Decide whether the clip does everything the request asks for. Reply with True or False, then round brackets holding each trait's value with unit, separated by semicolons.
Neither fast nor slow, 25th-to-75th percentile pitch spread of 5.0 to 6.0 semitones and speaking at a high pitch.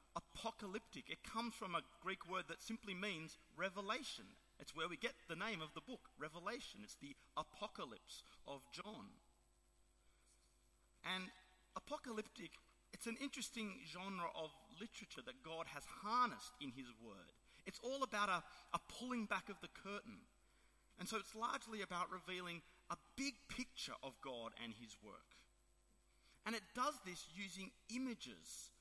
True (150 wpm; 5.3 semitones; 195 Hz)